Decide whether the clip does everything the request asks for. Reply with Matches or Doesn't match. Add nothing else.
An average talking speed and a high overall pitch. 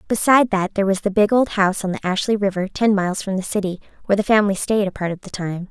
Doesn't match